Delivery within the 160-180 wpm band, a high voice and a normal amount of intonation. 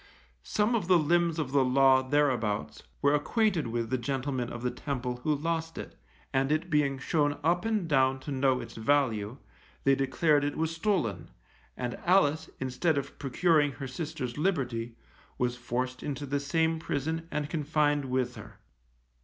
No: average, 165 wpm; medium, 140 Hz; average, 4.0 semitones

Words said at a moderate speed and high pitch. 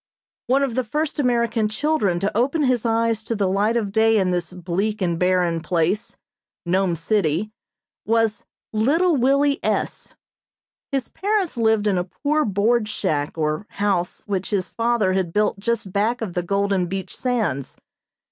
Yes: average, 160 wpm; high, 210 Hz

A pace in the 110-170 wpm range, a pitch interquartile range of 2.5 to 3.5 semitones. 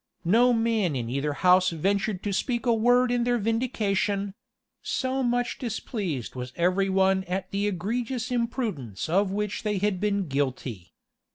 No: average, 155 wpm; average, 4.5 semitones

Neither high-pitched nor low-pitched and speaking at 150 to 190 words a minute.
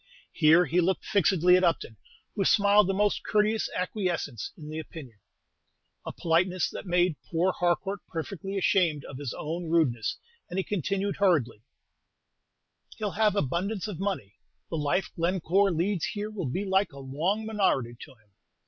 Yes: medium, 180 Hz; average, 155 wpm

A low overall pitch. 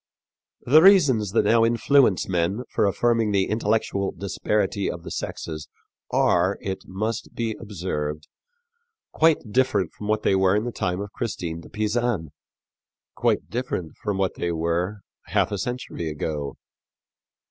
Yes: low, 100 Hz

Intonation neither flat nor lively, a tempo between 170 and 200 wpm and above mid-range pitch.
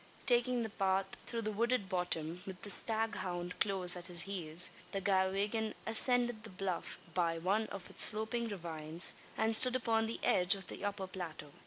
Yes: average, 3.8 semitones; average, 175 wpm; high, 195 Hz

